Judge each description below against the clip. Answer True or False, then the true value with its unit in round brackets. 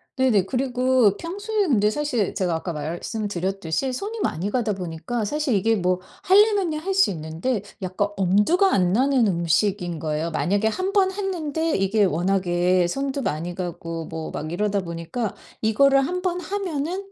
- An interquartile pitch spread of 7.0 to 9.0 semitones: True (8.5 semitones)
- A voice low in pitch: False (210 Hz)